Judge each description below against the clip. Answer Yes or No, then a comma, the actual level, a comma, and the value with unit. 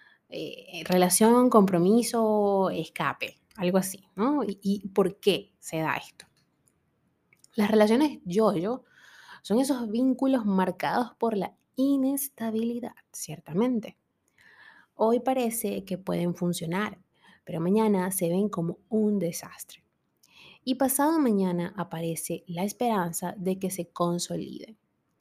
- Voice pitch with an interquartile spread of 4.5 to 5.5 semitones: Yes, average, 5.1 semitones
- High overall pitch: Yes, high, 205 Hz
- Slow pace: Yes, slow, 115 wpm